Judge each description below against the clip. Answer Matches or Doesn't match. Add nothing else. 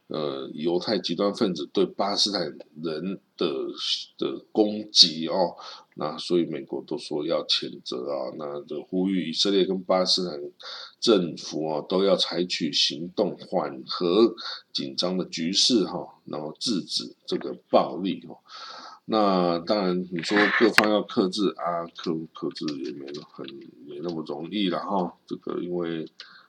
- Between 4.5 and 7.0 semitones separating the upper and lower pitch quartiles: Doesn't match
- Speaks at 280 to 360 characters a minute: Doesn't match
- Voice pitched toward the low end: Matches